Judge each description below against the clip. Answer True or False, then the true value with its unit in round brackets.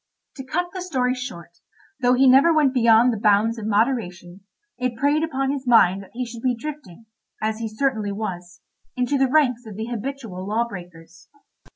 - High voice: True (235 Hz)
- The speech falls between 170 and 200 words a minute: True (185 wpm)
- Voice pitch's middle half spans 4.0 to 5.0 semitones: True (4.5 semitones)